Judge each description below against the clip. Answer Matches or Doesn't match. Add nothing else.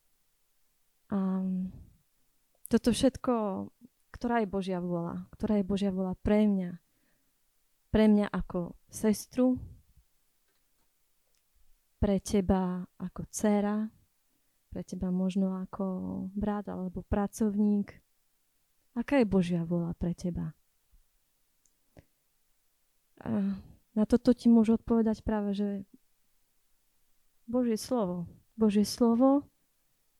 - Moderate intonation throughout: Matches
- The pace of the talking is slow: Matches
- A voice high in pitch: Matches